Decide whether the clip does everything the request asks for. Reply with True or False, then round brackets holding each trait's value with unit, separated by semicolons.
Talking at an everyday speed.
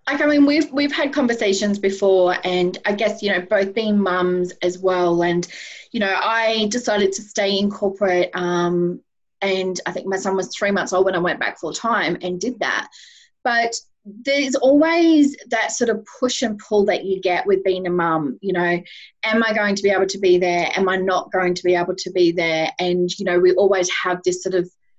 False (220 wpm)